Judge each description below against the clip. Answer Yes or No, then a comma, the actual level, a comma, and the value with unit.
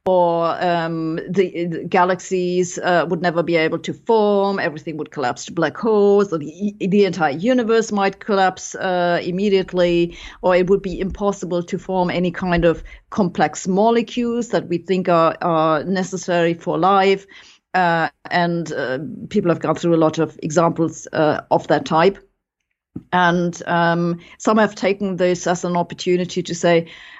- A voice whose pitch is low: No, medium, 180 Hz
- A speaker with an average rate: Yes, average, 160 wpm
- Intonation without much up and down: Yes, narrow, 2.3 semitones